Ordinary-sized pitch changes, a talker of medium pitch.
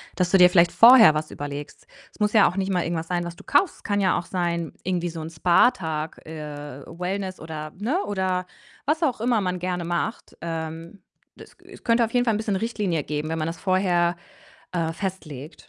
Yes: average, 3.7 semitones; medium, 180 Hz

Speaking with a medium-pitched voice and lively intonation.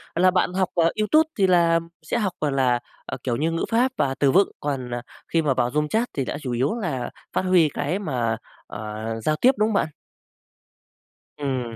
Yes: medium, 155 Hz; wide, 6.2 semitones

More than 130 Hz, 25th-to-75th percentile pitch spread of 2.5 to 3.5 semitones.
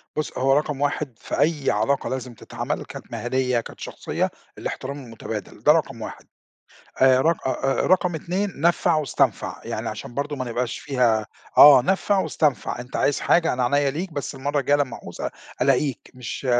Yes: medium, 140 Hz; average, 3.0 semitones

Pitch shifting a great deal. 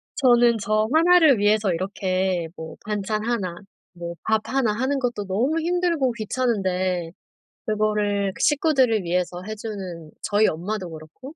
No: average, 5.0 semitones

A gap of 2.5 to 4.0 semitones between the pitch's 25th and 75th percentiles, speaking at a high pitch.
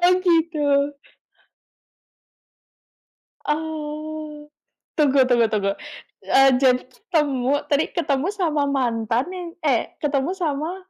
Yes: average, 2.9 semitones; very high, 290 Hz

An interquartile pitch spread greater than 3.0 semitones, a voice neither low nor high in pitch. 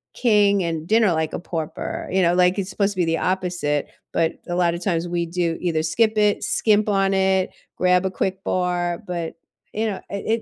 No: average, 2.7 semitones; medium, 180 Hz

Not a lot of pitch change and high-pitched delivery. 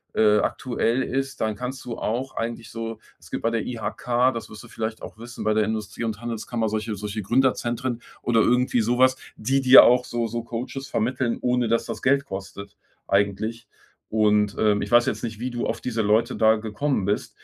No: narrow, 2.3 semitones; low, 115 Hz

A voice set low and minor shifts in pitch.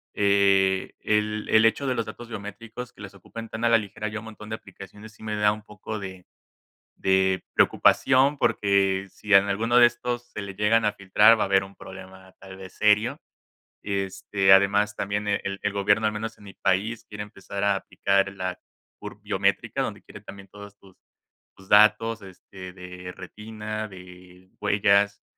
Yes: low, 100 Hz; narrow, 1.8 semitones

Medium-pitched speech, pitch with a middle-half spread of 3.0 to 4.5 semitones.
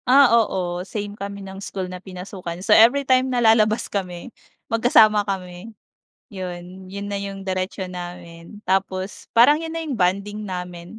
No: high, 195 Hz; average, 3.3 semitones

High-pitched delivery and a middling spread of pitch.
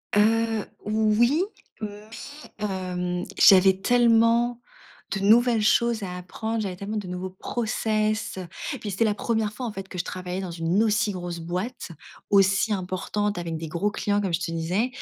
Yes: high, 205 Hz; average, 3.3 semitones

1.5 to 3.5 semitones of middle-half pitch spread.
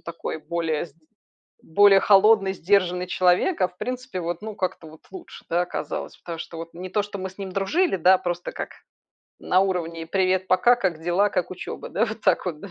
Yes: narrow, 2.6 semitones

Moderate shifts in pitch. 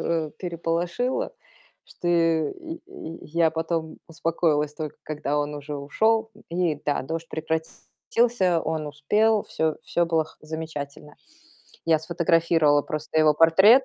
No: narrow, 2.1 semitones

